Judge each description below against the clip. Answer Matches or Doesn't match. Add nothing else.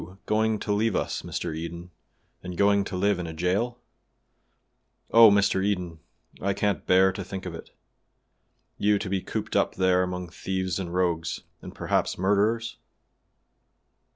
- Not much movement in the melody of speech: Matches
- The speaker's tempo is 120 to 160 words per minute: Matches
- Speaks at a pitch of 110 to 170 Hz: Doesn't match